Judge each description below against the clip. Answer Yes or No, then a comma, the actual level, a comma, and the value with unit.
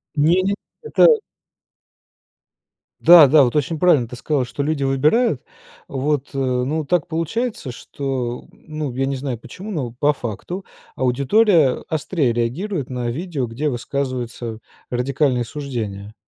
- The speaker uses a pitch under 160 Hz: Yes, medium, 140 Hz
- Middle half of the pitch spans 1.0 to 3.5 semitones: No, average, 4.2 semitones